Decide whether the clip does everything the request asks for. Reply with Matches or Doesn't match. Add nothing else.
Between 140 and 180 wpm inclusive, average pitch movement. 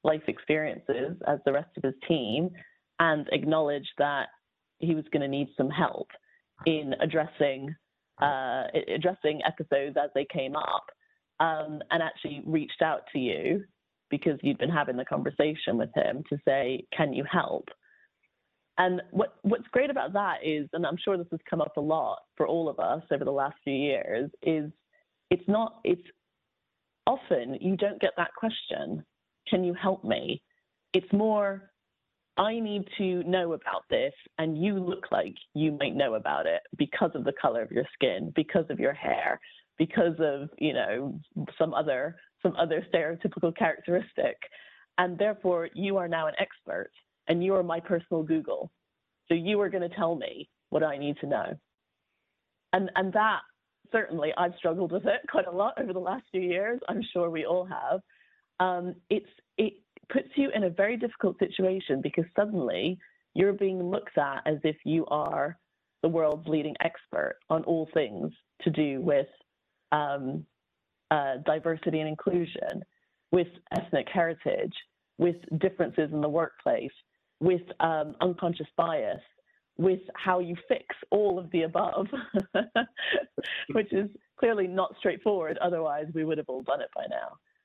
Matches